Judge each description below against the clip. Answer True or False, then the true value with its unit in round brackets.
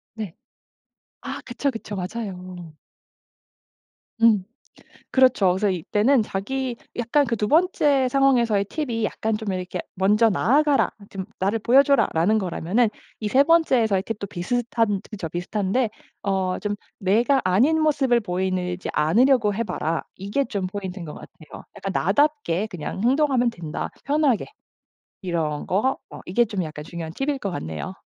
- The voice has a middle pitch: False (210 Hz)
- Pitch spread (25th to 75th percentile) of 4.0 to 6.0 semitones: True (5.5 semitones)